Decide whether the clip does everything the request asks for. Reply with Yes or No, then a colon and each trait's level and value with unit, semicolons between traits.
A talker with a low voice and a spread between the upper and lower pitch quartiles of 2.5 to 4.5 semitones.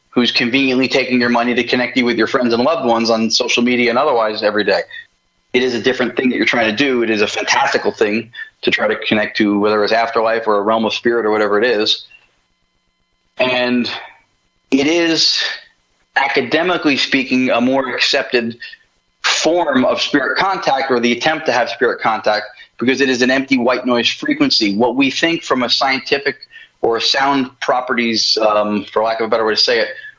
Yes: low, 125 Hz; average, 3.3 semitones